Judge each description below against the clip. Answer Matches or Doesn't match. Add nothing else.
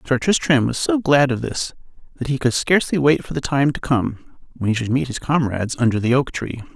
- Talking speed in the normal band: Doesn't match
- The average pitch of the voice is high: Doesn't match